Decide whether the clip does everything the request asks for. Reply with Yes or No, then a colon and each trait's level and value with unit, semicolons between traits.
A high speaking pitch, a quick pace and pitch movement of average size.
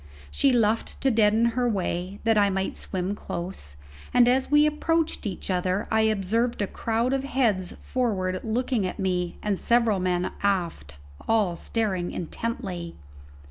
No: high, 210 Hz; average, 150 wpm; average, 4.3 semitones